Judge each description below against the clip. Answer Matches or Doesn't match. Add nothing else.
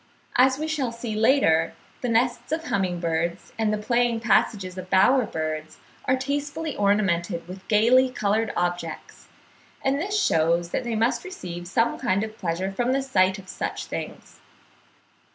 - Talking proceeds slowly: Doesn't match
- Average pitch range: Doesn't match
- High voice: Matches